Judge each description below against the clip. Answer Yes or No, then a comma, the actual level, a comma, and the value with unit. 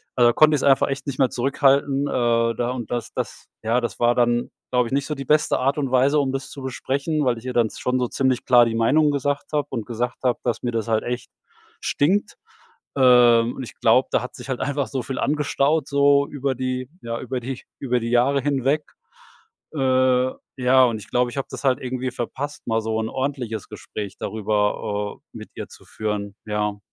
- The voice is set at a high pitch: No, low, 125 Hz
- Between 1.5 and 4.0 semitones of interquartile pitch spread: Yes, average, 2.7 semitones